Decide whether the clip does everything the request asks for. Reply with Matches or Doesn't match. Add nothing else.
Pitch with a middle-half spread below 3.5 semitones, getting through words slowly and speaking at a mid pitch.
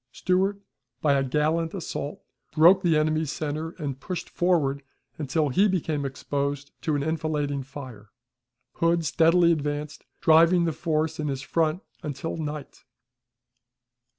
Matches